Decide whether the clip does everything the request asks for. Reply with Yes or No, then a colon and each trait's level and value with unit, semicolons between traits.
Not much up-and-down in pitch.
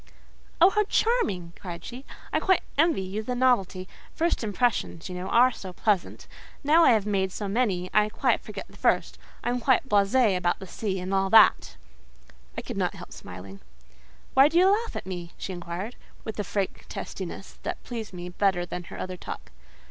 No: wide, 5.4 semitones